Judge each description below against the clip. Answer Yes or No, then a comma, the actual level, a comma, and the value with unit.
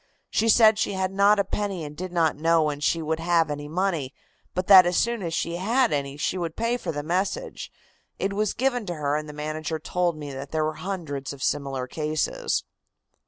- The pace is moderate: No, fast, 215 wpm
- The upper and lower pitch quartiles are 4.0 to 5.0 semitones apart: Yes, average, 4.5 semitones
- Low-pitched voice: No, medium, 165 Hz